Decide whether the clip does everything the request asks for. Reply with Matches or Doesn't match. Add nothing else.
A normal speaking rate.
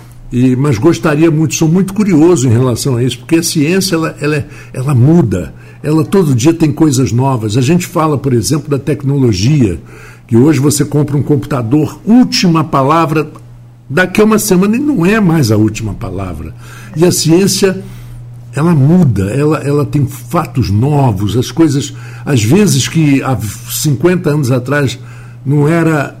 Matches